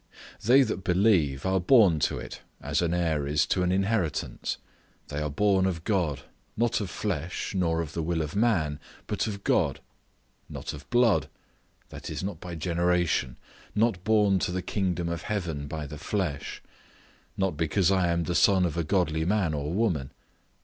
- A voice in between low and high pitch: No, very low, 90 Hz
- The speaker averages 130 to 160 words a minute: No, average, 175 wpm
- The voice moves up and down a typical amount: Yes, average, 3.9 semitones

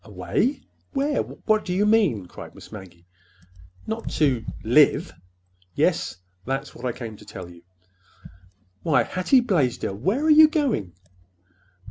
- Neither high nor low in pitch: Yes, medium, 160 Hz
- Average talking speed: No, slow, 130 wpm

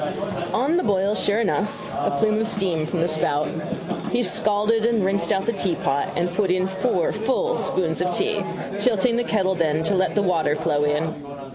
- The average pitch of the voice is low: No, high, 190 Hz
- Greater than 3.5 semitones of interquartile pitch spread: Yes, average, 4.8 semitones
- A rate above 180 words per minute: Yes, average, 190 wpm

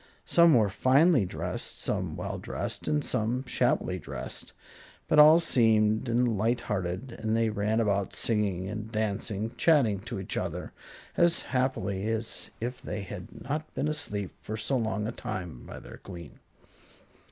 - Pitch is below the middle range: Yes, low, 110 Hz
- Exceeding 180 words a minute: No, average, 155 wpm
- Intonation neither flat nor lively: Yes, average, 3.9 semitones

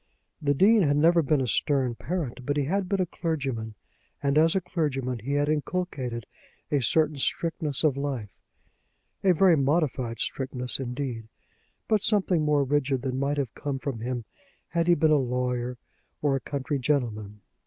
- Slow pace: No, average, 170 wpm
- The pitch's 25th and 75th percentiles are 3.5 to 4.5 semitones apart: Yes, average, 3.9 semitones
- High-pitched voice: No, medium, 140 Hz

